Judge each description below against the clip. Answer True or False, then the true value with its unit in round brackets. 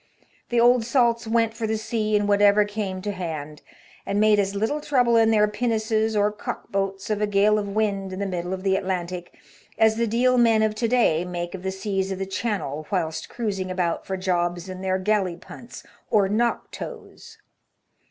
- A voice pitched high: True (205 Hz)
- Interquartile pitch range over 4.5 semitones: False (2.9 semitones)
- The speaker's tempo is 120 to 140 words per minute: False (200 wpm)